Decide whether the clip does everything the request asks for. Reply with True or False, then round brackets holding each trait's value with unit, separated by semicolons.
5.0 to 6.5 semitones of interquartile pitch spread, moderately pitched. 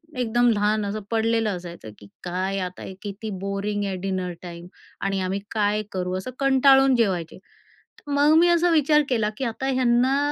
False (5.3 semitones; 215 Hz)